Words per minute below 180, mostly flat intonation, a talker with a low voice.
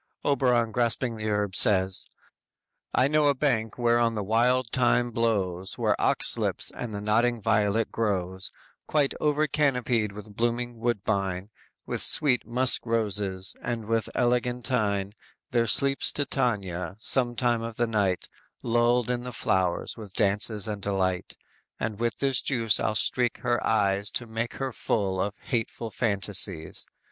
No: average, 145 wpm; average, 3.2 semitones; low, 115 Hz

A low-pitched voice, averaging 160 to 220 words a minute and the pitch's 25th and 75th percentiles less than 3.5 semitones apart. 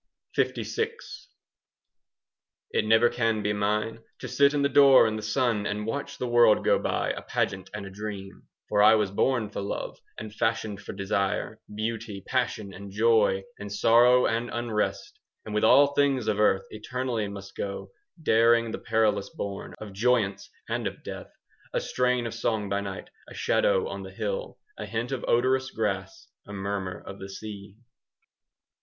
Yes: low, 110 Hz; average, 175 wpm; average, 3.0 semitones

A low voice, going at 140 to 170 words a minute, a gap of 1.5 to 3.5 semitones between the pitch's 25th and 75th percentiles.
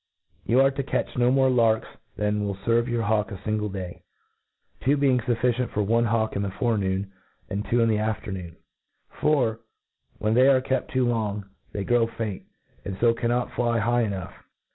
No: low, 115 Hz; average, 185 wpm; average, 2.9 semitones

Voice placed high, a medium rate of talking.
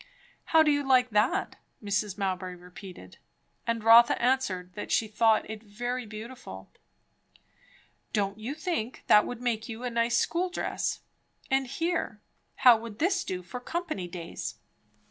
Yes: high, 230 Hz; average, 145 wpm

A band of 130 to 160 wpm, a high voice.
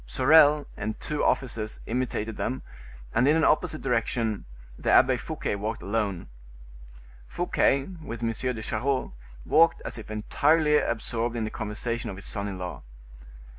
No: average, 150 wpm; low, 115 Hz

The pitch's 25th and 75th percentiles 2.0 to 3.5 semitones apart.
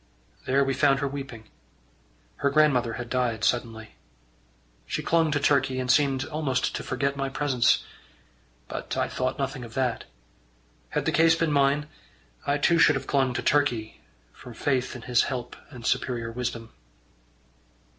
Yes: narrow, 2.6 semitones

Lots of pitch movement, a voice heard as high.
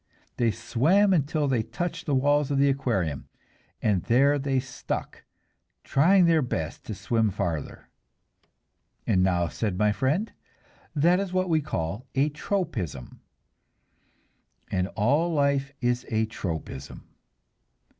No: wide, 6.3 semitones; low, 135 Hz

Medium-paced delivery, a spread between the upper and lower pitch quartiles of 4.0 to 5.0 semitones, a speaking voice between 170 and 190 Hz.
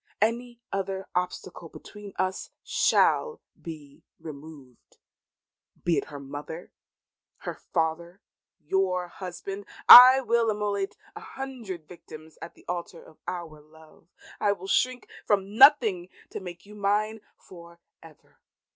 No: slow, 125 wpm; average, 4.3 semitones; medium, 185 Hz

